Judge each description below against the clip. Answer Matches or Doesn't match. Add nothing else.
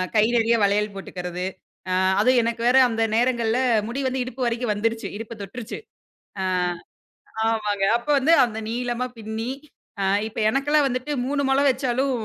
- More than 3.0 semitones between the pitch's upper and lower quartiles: Doesn't match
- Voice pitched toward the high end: Matches